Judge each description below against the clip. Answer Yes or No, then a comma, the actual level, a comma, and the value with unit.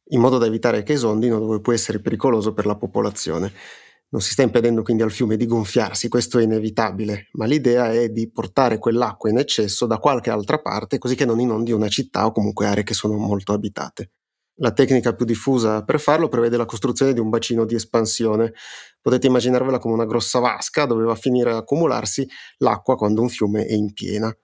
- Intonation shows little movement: Yes, narrow, 2.1 semitones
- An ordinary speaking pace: No, fast, 205 wpm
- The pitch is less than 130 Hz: Yes, low, 115 Hz